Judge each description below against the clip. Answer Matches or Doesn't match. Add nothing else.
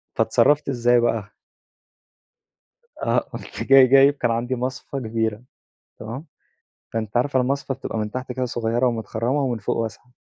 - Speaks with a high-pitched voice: Doesn't match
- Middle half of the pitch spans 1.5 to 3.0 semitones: Matches